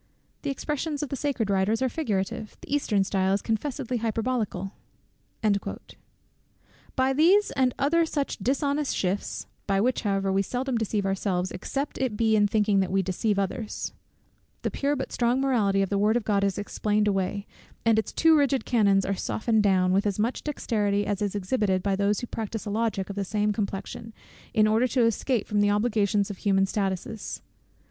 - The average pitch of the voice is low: No, high, 210 Hz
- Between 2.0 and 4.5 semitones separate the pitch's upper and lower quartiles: Yes, average, 4.1 semitones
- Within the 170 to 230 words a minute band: Yes, average, 185 wpm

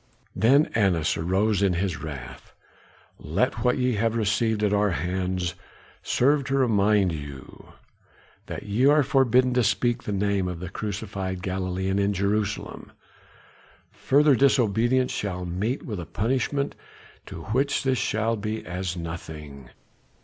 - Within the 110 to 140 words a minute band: Yes, slow, 135 wpm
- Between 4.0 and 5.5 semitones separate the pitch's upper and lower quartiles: Yes, average, 4.8 semitones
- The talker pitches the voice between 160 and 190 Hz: No, low, 100 Hz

